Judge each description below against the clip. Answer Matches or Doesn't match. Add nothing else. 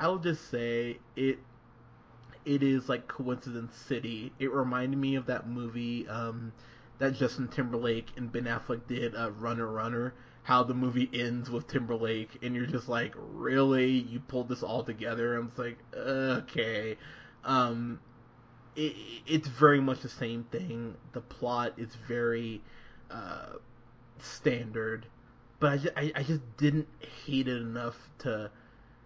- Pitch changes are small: Matches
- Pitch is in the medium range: Doesn't match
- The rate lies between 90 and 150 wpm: Matches